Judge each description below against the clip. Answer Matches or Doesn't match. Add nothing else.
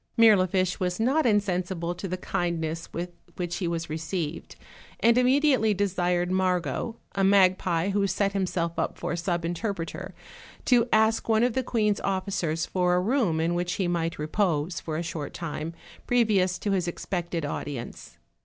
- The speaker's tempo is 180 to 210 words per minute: Doesn't match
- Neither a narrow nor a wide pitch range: Matches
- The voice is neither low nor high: Matches